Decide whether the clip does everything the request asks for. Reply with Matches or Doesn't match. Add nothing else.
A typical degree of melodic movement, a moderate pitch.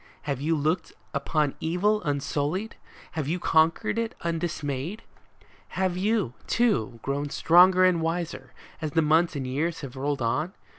Matches